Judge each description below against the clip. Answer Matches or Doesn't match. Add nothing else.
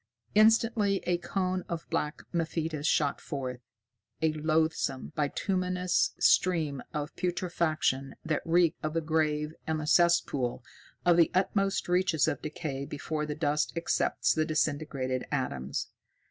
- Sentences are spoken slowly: Matches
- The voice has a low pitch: Doesn't match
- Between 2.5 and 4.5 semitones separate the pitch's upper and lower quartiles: Matches